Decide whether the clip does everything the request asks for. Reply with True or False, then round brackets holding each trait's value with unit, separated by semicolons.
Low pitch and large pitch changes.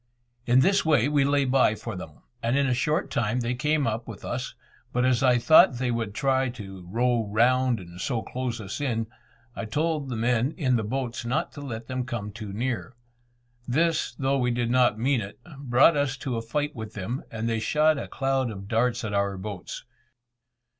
False (125 Hz; 3.2 semitones)